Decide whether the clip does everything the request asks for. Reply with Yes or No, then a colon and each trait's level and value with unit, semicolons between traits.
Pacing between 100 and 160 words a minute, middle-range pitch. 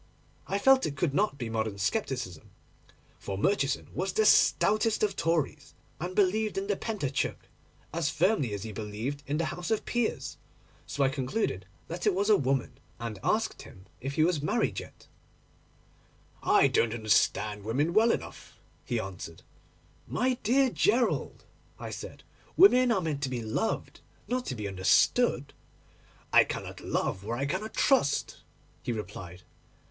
Yes: average, 155 wpm; medium, 145 Hz